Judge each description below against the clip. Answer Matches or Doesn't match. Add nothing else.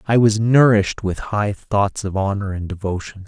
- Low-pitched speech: Matches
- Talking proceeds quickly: Doesn't match